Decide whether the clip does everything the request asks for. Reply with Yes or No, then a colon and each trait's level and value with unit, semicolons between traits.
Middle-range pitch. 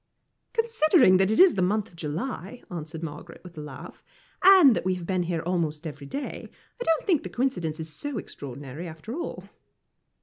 Yes: medium, 180 Hz